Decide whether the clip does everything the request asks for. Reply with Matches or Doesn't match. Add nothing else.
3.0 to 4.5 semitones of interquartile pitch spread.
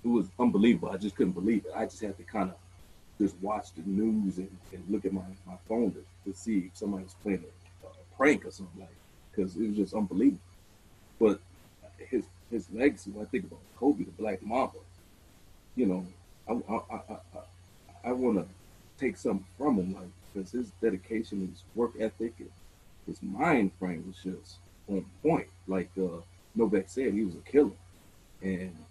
Doesn't match